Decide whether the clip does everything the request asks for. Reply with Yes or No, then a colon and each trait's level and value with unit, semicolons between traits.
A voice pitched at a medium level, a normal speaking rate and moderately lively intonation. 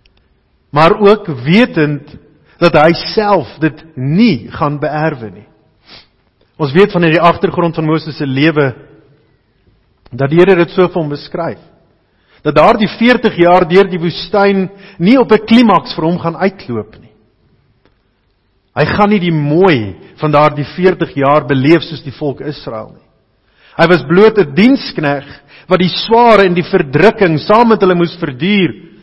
Yes: medium, 160 Hz; average, 155 wpm; average, 5.0 semitones